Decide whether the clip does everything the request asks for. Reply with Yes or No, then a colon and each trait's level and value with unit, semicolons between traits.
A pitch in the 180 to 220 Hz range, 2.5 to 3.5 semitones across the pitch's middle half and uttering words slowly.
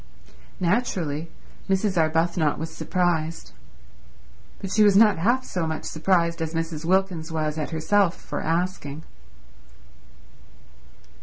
No: medium, 170 Hz; average, 3.0 semitones; slow, 110 wpm